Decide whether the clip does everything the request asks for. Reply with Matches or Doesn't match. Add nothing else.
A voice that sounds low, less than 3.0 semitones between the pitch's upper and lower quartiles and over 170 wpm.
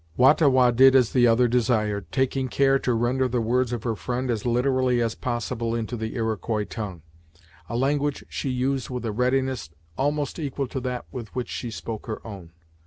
Matches